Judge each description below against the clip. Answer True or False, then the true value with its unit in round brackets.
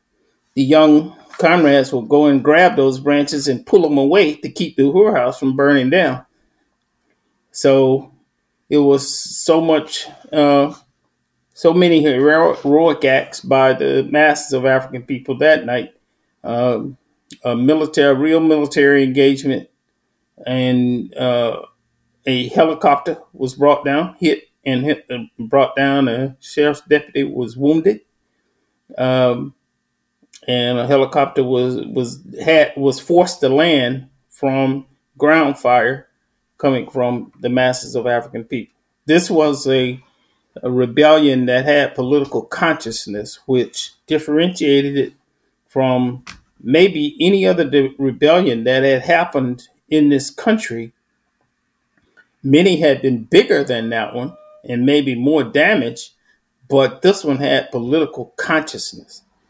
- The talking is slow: True (125 wpm)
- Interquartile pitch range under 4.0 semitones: True (3.0 semitones)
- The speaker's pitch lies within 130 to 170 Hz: True (140 Hz)